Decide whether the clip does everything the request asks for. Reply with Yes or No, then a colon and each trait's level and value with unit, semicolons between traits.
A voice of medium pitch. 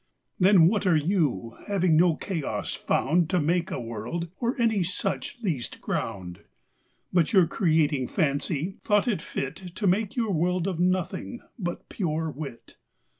Yes: medium, 175 Hz